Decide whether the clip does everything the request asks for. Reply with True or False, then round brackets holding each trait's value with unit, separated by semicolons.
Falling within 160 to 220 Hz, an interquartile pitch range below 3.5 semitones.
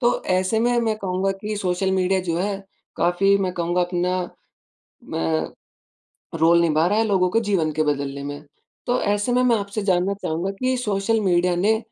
True (190 Hz; 3.1 semitones)